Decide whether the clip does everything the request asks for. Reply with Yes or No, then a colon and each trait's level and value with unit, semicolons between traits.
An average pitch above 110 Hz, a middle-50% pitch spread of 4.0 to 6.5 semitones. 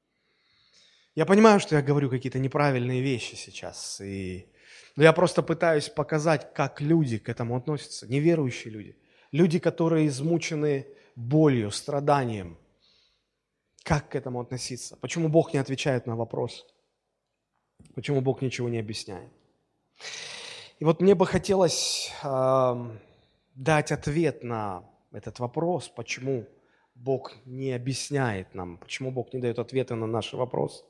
Yes: low, 135 Hz; average, 4.8 semitones